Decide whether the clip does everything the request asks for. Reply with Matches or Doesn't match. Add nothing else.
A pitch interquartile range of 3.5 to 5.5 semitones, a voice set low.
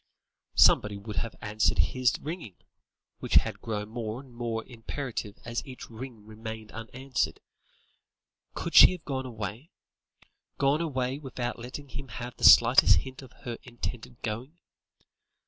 Doesn't match